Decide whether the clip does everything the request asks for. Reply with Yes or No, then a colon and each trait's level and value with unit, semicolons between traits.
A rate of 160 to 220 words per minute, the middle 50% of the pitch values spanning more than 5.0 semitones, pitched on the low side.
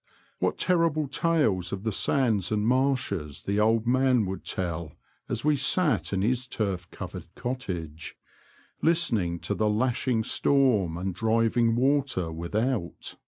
No: slow, 135 wpm; wide, 5.6 semitones; low, 115 Hz